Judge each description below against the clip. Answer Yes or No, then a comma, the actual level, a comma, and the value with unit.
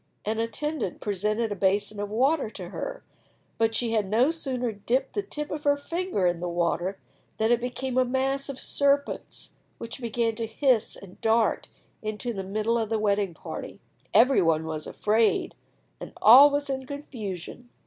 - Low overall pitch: No, high, 230 Hz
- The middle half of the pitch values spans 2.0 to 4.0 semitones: No, average, 4.6 semitones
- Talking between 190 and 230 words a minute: No, average, 175 wpm